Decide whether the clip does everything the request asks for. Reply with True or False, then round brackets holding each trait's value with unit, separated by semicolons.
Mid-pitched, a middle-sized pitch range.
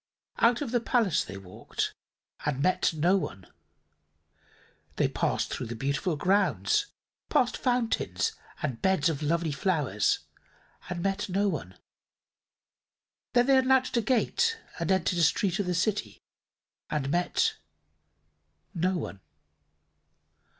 False (180 Hz; 7.1 semitones)